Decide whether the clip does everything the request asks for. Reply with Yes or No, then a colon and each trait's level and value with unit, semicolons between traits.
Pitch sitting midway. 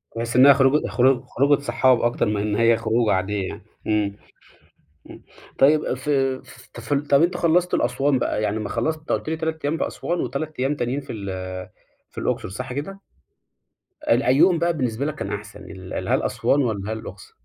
No: low, 130 Hz